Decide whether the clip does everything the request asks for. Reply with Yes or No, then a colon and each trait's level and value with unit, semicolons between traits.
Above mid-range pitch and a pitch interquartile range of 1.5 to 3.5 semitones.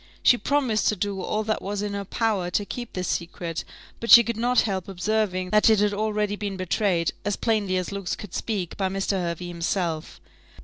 Yes: high, 200 Hz; average, 2.8 semitones